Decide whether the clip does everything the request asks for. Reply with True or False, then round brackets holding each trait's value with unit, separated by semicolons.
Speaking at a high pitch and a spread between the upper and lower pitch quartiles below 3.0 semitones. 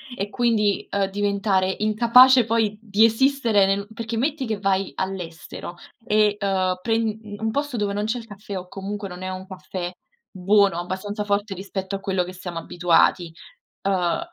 True (200 Hz; 2.6 semitones)